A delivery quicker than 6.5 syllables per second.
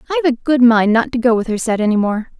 Yes: 6.8 syllables/s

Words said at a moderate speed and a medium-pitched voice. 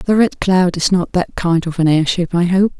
No: fast, 255 wpm; medium, 180 Hz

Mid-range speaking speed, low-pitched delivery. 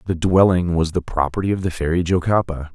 Yes: average, 195 wpm; very low, 90 Hz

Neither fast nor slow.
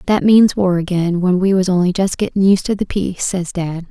No: fast, 245 wpm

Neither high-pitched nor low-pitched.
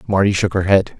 No: low, 100 Hz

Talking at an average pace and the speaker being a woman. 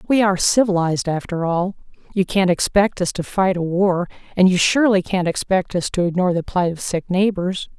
Yes: average, 195 wpm; female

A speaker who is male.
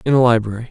Yes: male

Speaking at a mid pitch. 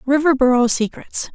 No: very high, 265 Hz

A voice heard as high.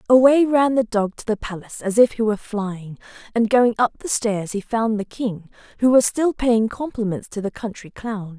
Yes: high, 220 Hz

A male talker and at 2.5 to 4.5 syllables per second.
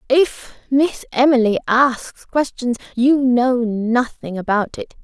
No: female; 3.5 syllables/s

